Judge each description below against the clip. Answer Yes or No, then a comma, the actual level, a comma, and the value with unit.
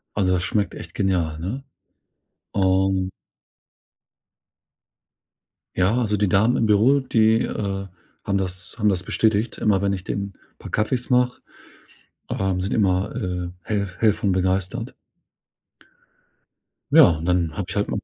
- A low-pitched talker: Yes, very low, 95 Hz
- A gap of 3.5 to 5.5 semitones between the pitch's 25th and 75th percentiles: No, narrow, 2.6 semitones